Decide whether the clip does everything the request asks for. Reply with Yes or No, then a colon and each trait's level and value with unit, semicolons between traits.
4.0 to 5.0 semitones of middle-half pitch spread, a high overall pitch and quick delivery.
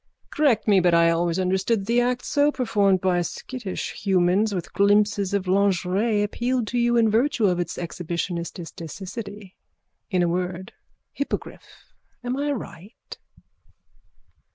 No: average, 4.5 semitones; high, 200 Hz; slow, 135 wpm